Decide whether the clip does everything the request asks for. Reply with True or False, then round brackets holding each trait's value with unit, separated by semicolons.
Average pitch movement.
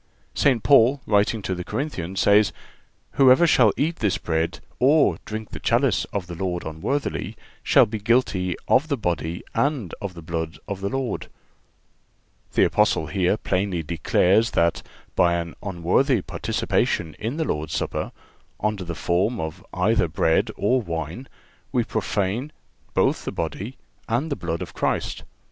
False (6.2 semitones)